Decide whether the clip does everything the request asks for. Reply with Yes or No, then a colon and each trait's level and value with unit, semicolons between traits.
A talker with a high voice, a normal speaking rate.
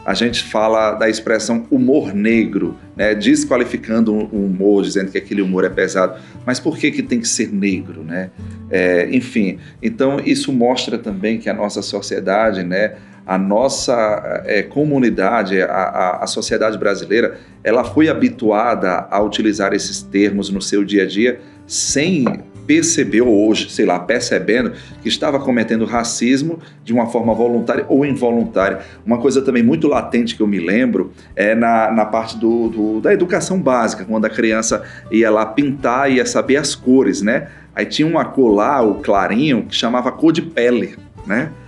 No: low, 115 Hz; average, 170 wpm